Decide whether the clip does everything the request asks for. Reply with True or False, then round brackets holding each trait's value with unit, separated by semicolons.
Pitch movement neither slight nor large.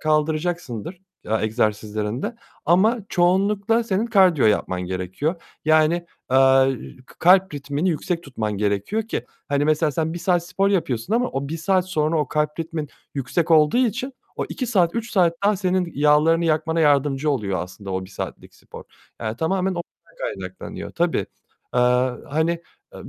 False (5.9 semitones)